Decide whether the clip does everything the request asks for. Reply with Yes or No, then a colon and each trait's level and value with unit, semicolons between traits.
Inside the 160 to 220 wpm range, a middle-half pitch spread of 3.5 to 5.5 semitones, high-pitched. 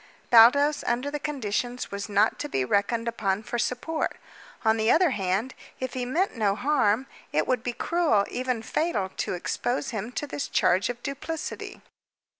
Yes: average, 170 wpm; average, 5.1 semitones; high, 240 Hz